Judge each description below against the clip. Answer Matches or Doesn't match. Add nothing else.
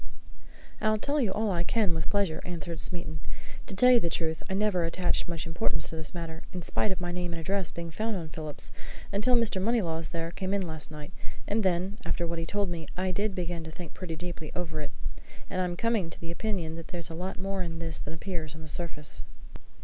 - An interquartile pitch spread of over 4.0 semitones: Doesn't match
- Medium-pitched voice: Matches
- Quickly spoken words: Matches